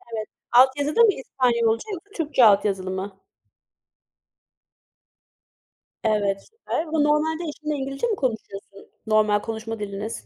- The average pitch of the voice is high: Yes, high, 235 Hz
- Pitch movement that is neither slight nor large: No, wide, 6.4 semitones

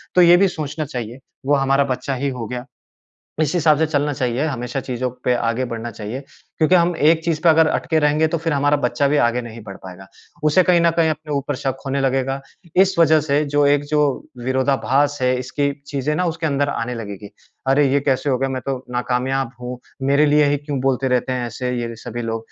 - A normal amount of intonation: Yes, average, 3.4 semitones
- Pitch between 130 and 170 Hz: Yes, medium, 140 Hz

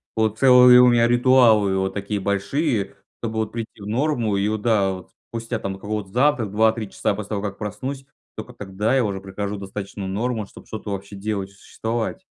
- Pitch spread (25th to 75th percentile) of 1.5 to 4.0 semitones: Yes, average, 3.1 semitones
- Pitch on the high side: No, low, 110 Hz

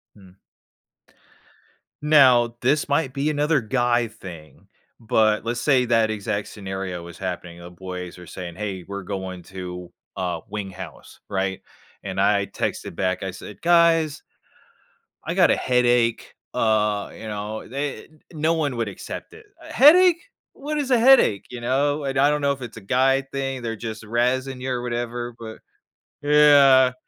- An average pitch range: No, wide, 6.0 semitones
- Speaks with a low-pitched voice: Yes, low, 120 Hz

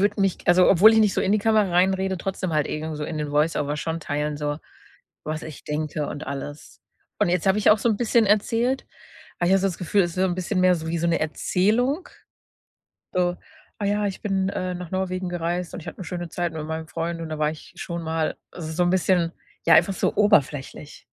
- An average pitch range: Yes, average, 3.4 semitones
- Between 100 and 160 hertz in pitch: No, medium, 175 Hz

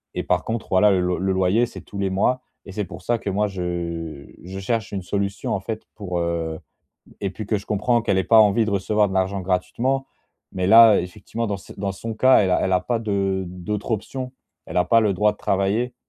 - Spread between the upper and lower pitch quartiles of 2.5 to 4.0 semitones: Yes, average, 2.9 semitones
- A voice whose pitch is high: No, low, 100 Hz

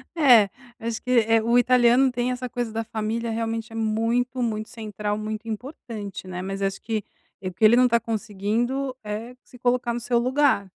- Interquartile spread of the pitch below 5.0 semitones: Yes, narrow, 2.4 semitones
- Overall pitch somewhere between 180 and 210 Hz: No, high, 230 Hz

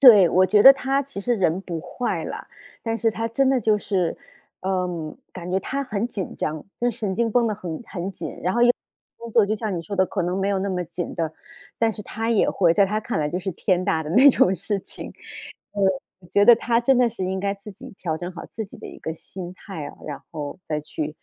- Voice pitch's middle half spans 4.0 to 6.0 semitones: Yes, average, 4.3 semitones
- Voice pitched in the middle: No, high, 195 Hz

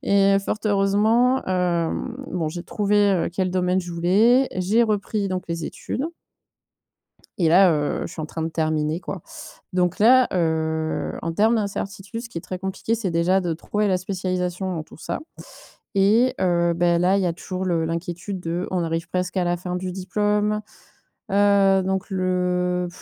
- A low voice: No, medium, 185 Hz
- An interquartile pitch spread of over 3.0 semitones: No, average, 2.7 semitones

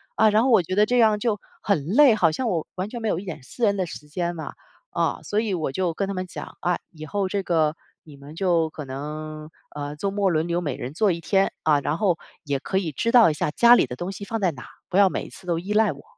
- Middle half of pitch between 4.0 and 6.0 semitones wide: Yes, average, 4.9 semitones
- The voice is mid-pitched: Yes, medium, 180 Hz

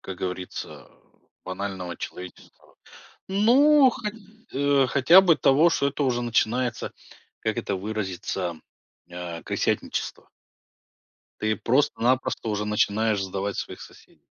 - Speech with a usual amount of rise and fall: No, wide, 6.7 semitones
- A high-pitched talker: No, low, 110 Hz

